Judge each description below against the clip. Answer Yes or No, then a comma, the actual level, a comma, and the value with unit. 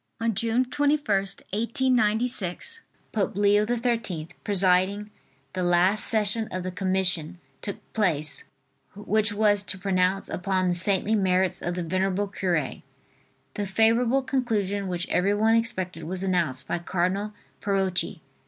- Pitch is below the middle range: No, high, 195 Hz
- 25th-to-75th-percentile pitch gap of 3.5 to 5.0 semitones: No, average, 3.1 semitones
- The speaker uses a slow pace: Yes, slow, 125 wpm